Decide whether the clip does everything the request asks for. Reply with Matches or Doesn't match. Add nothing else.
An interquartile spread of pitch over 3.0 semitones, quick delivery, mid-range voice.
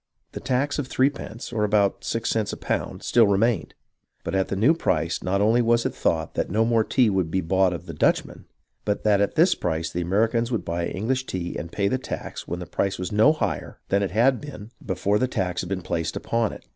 Doesn't match